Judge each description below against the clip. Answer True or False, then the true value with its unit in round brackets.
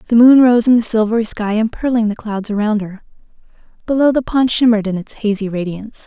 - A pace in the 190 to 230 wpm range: True (200 wpm)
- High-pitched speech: True (220 Hz)